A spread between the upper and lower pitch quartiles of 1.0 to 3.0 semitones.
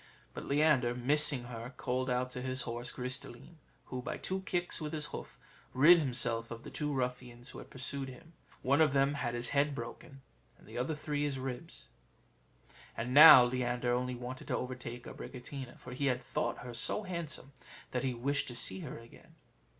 Yes: average, 2.7 semitones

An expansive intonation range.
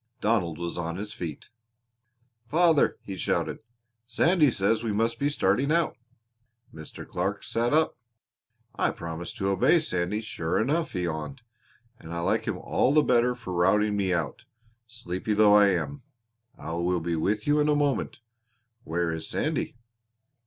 Yes: wide, 6.3 semitones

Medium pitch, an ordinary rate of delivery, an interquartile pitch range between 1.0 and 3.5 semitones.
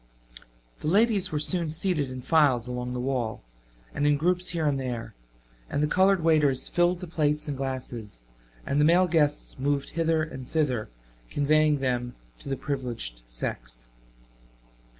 No: medium, 145 Hz; average, 155 wpm; average, 4.4 semitones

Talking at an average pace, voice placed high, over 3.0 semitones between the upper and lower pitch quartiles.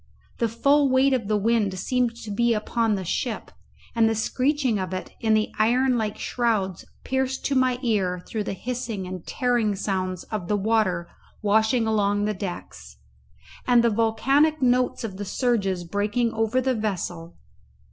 Yes: average, 165 wpm; high, 220 Hz; average, 3.6 semitones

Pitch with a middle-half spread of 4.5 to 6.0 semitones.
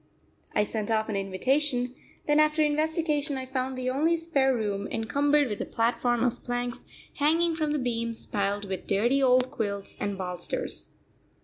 Yes: average, 5.2 semitones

